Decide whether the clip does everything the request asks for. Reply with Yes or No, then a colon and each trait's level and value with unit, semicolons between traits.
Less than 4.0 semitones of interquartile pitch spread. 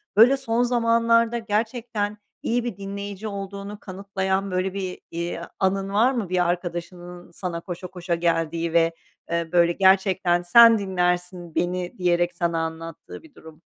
Yes: average, 3.1 semitones